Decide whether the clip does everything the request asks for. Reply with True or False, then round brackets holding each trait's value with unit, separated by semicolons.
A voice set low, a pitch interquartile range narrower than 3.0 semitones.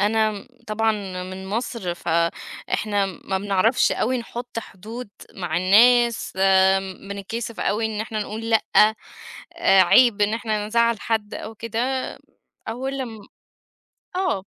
False (220 Hz; 2.6 semitones)